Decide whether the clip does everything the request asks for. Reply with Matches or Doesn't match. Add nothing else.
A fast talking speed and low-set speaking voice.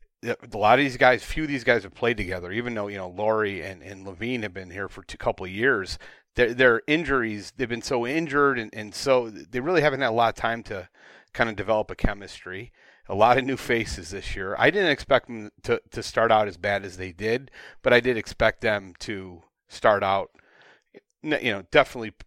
Matches